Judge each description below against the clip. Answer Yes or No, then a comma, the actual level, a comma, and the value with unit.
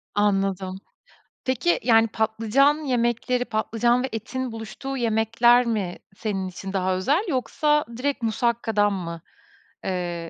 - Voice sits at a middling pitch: No, high, 225 Hz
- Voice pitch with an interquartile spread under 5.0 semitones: Yes, average, 4.1 semitones